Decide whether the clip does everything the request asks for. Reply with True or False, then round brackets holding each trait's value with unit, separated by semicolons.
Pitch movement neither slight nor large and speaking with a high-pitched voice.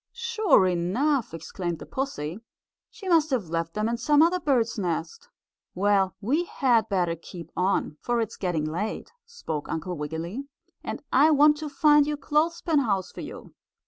False (9.0 semitones; 230 Hz)